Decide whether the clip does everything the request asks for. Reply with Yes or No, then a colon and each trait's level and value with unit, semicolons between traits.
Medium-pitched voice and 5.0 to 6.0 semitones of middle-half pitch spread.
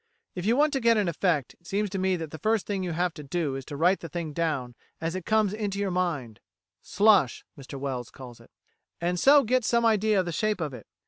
Yes: medium, 180 Hz; wide, 5.6 semitones